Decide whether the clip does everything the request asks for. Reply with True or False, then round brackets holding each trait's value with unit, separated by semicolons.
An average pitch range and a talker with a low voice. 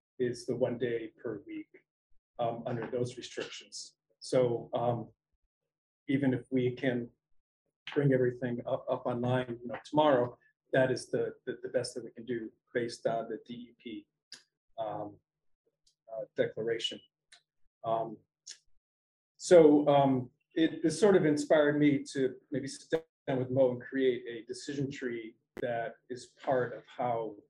True (4.0 semitones; 130 Hz)